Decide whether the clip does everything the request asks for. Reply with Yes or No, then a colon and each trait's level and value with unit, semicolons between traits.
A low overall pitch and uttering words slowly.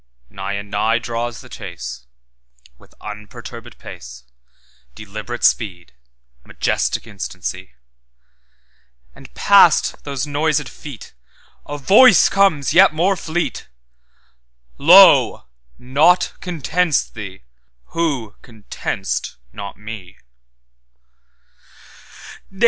Yes: low, 105 Hz; slow, 70 wpm